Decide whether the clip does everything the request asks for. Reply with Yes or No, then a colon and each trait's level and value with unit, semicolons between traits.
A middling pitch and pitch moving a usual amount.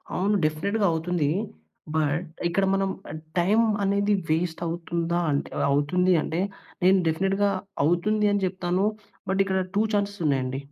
Yes: medium, 180 Hz; average, 3.5 semitones